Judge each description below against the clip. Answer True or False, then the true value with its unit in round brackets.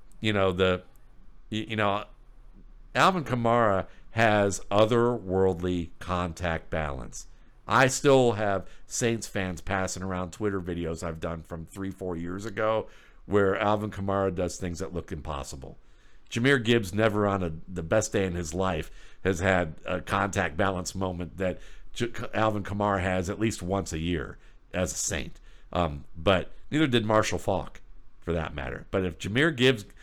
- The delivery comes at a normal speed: True (155 wpm)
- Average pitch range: True (3.7 semitones)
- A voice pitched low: True (95 Hz)